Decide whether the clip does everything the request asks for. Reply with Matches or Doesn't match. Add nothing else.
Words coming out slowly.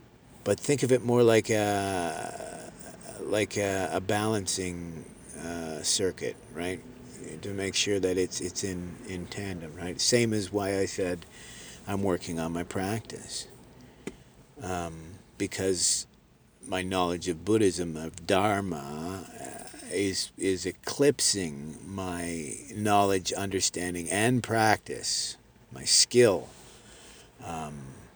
Matches